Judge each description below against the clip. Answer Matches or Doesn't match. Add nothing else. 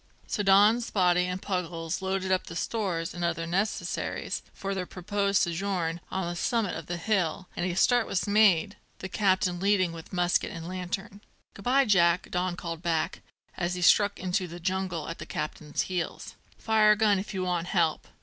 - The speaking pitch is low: Doesn't match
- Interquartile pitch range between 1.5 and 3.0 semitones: Matches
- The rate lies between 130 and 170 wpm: Doesn't match